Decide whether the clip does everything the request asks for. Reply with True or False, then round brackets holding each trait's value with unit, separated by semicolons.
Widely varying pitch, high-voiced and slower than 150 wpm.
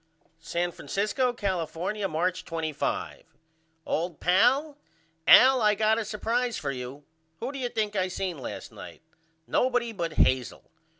True (6.0 semitones; 195 Hz; 135 wpm)